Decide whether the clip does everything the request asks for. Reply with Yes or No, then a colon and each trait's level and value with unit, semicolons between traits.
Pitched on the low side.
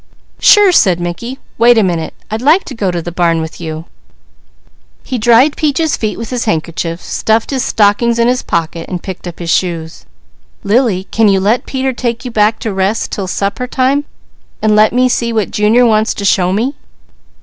No: high, 215 Hz